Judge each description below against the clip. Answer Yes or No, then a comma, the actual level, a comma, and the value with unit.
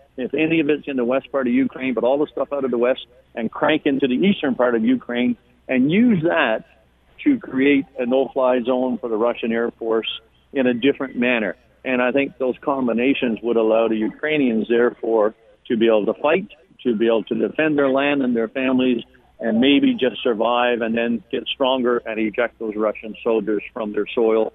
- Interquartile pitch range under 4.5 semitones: Yes, average, 3.2 semitones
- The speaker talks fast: Yes, fast, 210 wpm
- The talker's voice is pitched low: Yes, low, 125 Hz